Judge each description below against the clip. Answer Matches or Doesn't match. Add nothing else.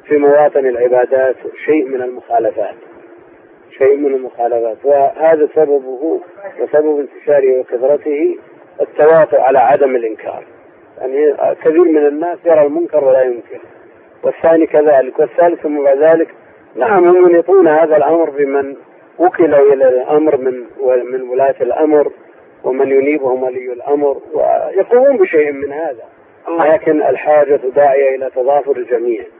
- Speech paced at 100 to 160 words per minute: Matches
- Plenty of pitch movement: Matches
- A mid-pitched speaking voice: Matches